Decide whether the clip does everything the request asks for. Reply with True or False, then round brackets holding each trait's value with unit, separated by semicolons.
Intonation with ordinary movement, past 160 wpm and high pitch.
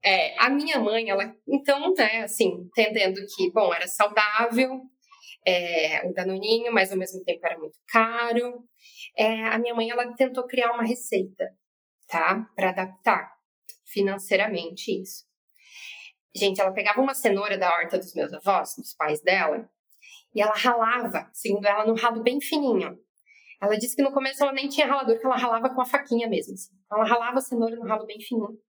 True (4.2 semitones; 175 wpm; 225 Hz)